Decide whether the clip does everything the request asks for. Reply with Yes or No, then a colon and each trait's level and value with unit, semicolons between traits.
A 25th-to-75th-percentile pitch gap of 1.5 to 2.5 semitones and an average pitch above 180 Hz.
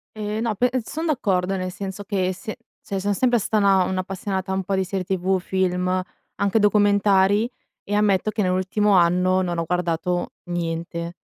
Yes: narrow, 2.1 semitones; high, 190 Hz